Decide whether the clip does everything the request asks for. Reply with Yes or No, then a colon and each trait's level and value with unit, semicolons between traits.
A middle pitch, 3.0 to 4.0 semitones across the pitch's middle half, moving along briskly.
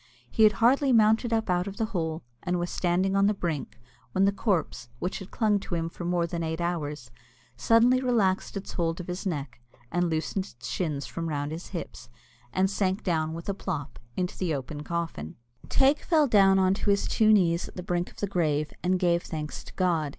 Yes: medium, 180 Hz; average, 3.6 semitones; fast, 210 wpm